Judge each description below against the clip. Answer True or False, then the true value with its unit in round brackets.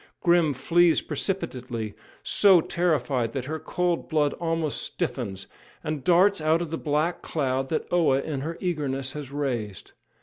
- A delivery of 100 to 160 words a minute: True (155 wpm)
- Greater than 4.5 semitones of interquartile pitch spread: False (4.2 semitones)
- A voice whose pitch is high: False (155 Hz)